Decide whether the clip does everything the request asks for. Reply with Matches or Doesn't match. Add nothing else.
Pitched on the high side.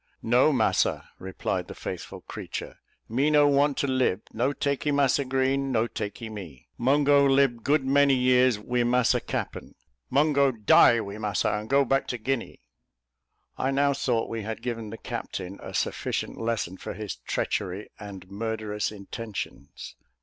Doesn't match